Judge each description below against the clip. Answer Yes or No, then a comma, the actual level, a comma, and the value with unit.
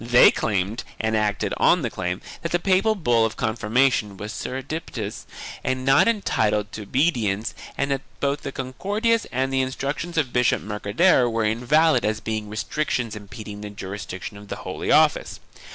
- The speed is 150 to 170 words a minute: Yes, average, 165 wpm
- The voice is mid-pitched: No, low, 120 Hz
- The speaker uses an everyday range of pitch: Yes, average, 4.7 semitones